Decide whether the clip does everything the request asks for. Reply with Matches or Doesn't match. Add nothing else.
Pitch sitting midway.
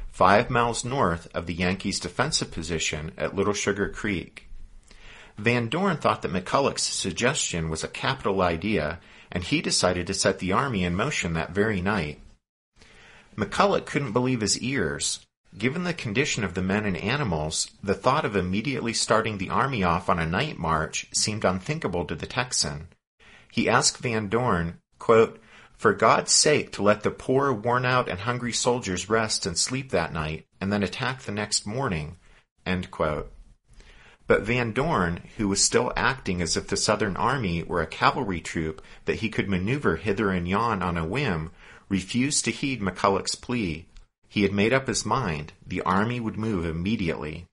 Doesn't match